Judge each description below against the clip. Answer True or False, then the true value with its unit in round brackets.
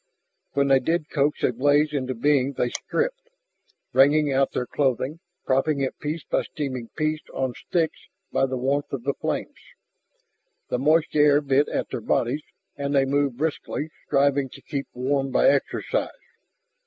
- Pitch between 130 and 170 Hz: True (140 Hz)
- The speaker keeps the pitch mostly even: True (2.1 semitones)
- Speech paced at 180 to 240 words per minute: False (160 wpm)